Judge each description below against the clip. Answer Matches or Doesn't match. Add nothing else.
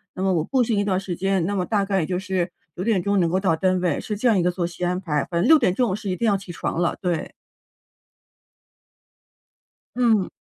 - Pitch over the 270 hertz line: Doesn't match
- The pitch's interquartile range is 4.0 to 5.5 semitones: Doesn't match